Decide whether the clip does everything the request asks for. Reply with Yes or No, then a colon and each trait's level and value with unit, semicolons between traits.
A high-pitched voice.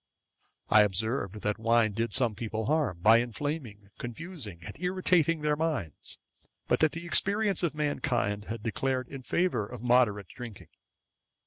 No: low, 120 Hz